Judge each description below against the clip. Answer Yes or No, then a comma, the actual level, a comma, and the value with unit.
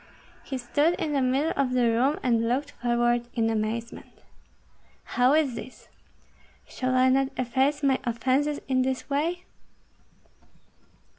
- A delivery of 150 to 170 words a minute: No, slow, 135 wpm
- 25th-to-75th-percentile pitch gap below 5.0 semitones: Yes, average, 2.7 semitones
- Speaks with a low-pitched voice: No, very high, 255 Hz